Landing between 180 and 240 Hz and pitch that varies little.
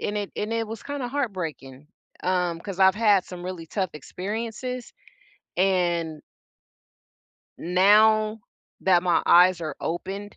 No: high, 190 Hz; average, 3.6 semitones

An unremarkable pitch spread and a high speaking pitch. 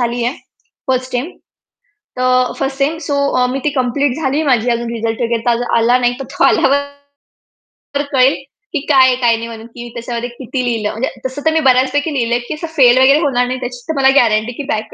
No: narrow, 2.3 semitones; very high, 255 Hz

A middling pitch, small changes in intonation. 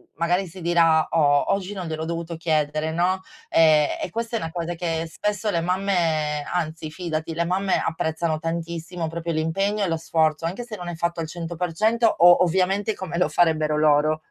Yes: medium, 170 Hz; narrow, 2.2 semitones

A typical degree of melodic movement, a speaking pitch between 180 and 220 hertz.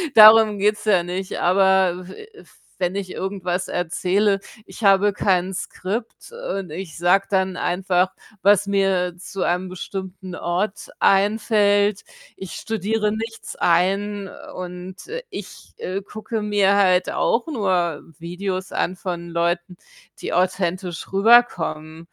No: narrow, 2.3 semitones; high, 190 Hz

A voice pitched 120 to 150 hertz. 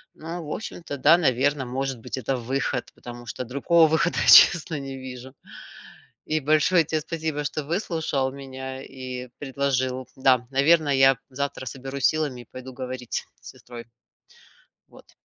Yes: low, 135 Hz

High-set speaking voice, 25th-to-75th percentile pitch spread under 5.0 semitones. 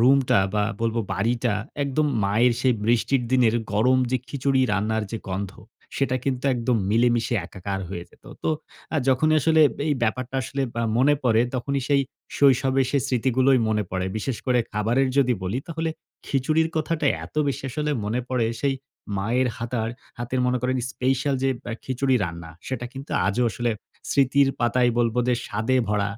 No: low, 125 Hz; average, 3.0 semitones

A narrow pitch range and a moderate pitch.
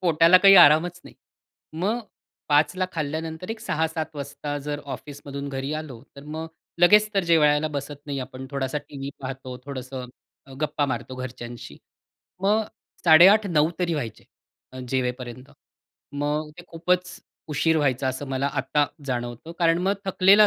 No: average, 3.8 semitones; medium, 150 Hz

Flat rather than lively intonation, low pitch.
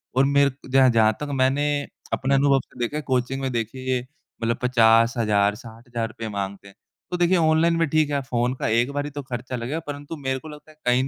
No: average, 3.5 semitones; low, 130 Hz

